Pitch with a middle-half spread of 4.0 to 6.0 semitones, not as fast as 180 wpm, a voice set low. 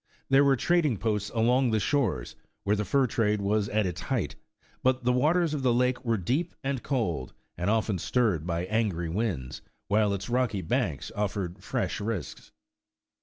Yes: average, 4.4 semitones; average, 170 wpm; low, 110 Hz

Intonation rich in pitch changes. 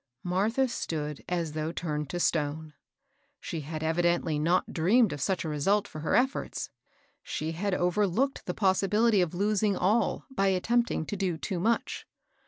No: average, 4.4 semitones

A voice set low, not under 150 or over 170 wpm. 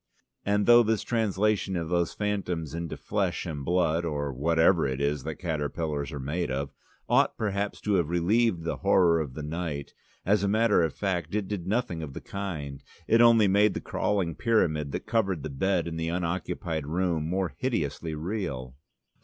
No: very low, 85 Hz; average, 180 wpm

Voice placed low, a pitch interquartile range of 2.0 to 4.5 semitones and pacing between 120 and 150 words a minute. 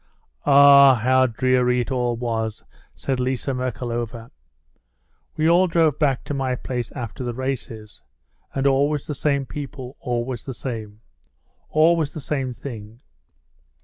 Yes: low, 130 Hz; average, 2.8 semitones; slow, 135 wpm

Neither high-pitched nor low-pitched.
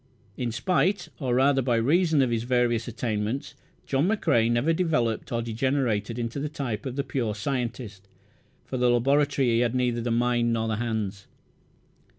No: low, 120 Hz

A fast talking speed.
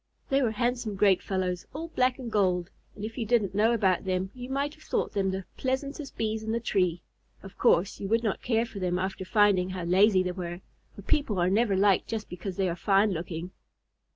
Yes: fast, 220 wpm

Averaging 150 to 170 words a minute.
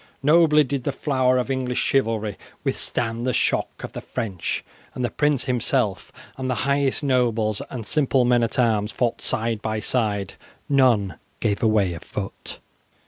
Yes: average, 160 wpm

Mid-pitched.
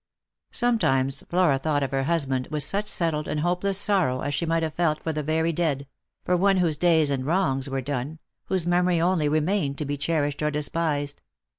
Yes: medium, 155 Hz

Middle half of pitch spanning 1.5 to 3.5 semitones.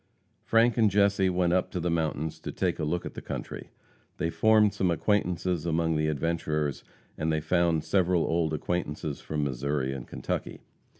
Yes: average, 3.0 semitones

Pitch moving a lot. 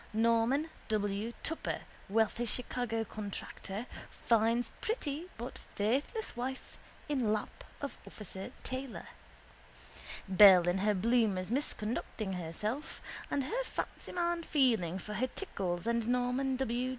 No: average, 4.2 semitones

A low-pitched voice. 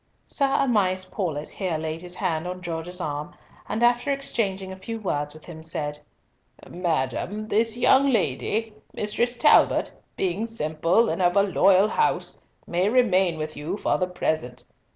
No: medium, 185 Hz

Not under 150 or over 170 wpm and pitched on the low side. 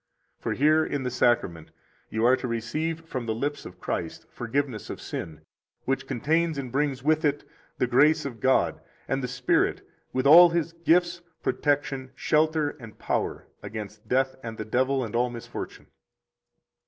Yes: average, 165 wpm; low, 130 Hz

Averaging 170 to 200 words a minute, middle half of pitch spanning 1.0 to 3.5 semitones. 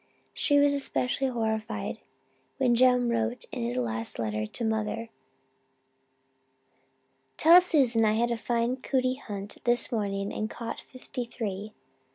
No: slow, 135 wpm; average, 3.1 semitones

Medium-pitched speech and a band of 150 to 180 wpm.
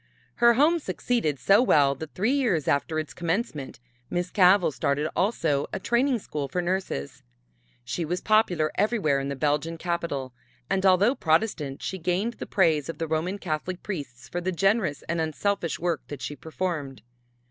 Yes: medium, 170 Hz; average, 170 wpm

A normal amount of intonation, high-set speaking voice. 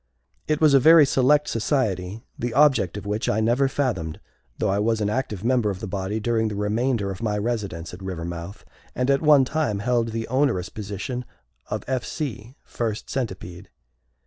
No: average, 4.4 semitones; low, 110 Hz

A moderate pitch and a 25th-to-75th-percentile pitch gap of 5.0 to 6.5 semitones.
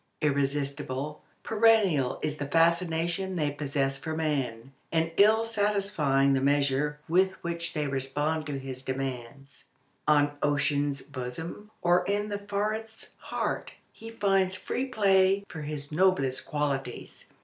Yes: medium, 150 Hz; wide, 5.5 semitones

